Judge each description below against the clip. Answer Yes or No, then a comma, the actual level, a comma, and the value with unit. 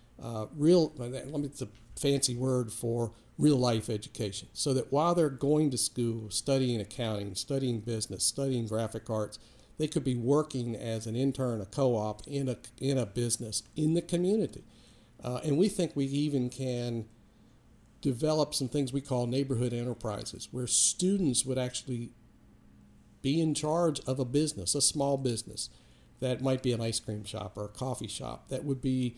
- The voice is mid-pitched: No, low, 125 Hz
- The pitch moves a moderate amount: Yes, average, 3.5 semitones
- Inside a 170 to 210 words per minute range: Yes, average, 175 wpm